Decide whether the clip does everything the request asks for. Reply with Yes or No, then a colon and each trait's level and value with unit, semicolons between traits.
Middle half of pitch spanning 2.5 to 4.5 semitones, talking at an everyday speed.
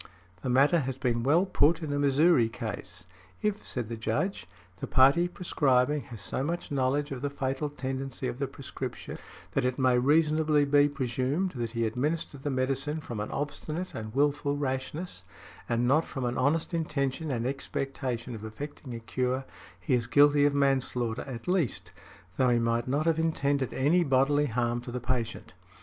Yes: average, 3.1 semitones; average, 175 wpm